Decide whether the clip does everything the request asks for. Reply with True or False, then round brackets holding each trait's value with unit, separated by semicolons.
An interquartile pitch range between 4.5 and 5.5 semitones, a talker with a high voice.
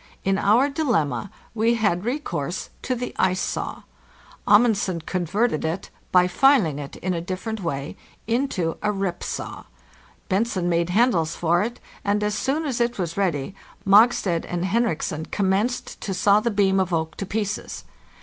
True (4.8 semitones; 195 Hz)